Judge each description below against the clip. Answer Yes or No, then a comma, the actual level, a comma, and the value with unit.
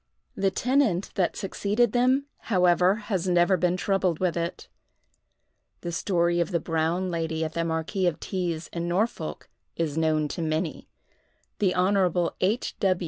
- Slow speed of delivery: No, average, 145 wpm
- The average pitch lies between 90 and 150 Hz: No, medium, 180 Hz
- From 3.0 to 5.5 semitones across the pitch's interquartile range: No, narrow, 2.6 semitones